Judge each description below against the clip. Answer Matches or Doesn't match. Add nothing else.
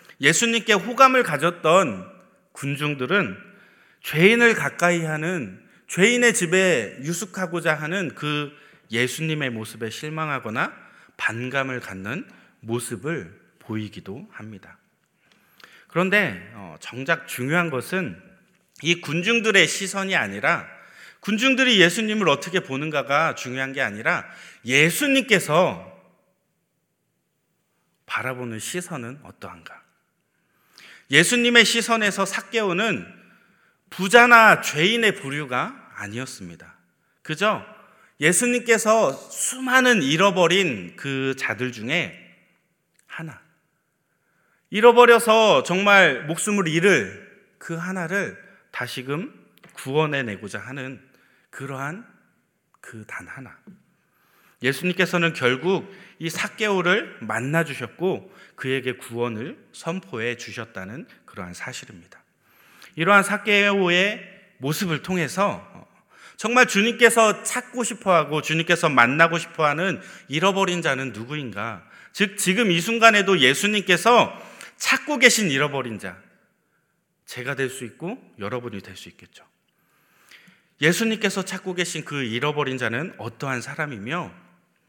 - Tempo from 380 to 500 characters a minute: Doesn't match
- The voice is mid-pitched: Matches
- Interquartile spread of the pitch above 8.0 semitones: Doesn't match